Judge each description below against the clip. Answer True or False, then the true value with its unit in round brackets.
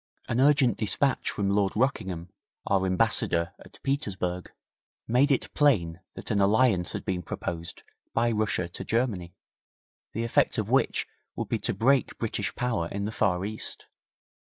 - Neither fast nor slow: True (150 wpm)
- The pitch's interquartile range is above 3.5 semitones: True (4.8 semitones)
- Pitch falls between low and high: False (105 Hz)